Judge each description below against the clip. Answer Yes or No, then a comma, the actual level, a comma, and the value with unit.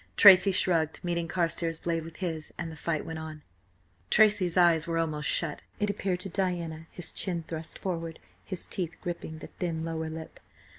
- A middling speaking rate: Yes, average, 180 wpm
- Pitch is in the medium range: Yes, medium, 165 Hz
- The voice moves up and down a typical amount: No, narrow, 2.0 semitones